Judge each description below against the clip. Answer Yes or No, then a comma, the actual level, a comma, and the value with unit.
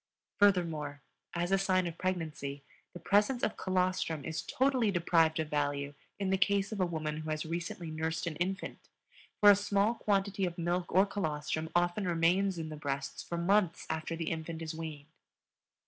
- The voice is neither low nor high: Yes, medium, 170 Hz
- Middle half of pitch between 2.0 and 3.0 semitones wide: No, average, 3.5 semitones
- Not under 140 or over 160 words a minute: No, average, 180 wpm